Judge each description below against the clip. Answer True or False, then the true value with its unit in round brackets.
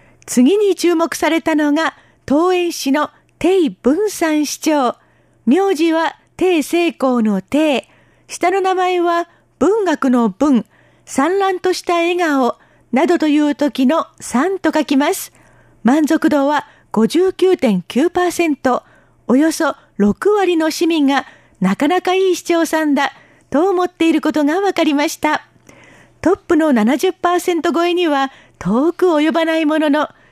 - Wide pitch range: False (3.6 semitones)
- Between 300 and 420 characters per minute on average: False (215 characters per minute)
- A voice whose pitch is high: True (320 Hz)